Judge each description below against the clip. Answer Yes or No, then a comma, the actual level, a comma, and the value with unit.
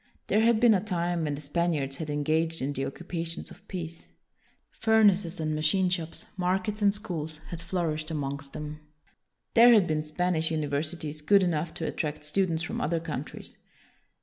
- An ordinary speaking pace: Yes, average, 170 wpm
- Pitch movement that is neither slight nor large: Yes, average, 3.2 semitones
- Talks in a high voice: No, medium, 165 Hz